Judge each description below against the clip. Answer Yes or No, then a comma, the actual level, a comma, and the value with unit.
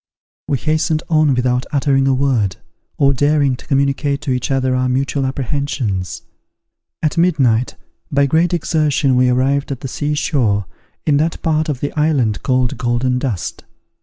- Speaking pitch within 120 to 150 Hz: Yes, low, 135 Hz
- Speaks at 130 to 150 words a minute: No, average, 160 wpm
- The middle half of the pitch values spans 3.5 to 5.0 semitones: No, average, 2.8 semitones